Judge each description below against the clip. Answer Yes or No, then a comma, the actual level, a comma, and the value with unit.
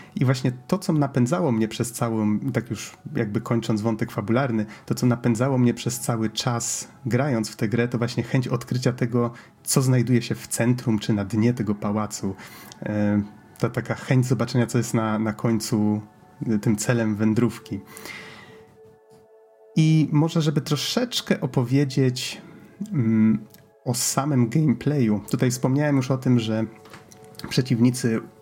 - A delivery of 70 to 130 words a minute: No, average, 145 wpm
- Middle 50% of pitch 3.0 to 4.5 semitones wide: Yes, average, 3.4 semitones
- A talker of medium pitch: No, low, 120 Hz